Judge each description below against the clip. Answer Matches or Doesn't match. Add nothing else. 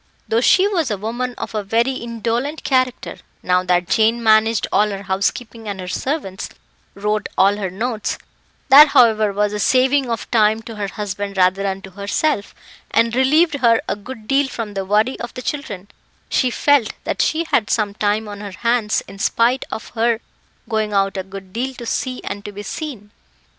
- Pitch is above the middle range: Matches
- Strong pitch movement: Doesn't match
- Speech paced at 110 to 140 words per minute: Doesn't match